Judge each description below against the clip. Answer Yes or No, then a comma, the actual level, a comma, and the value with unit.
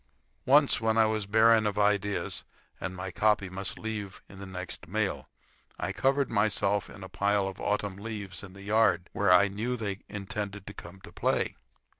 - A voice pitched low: Yes, low, 100 Hz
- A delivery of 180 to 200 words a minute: Yes, average, 185 wpm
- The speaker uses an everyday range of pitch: No, narrow, 2.1 semitones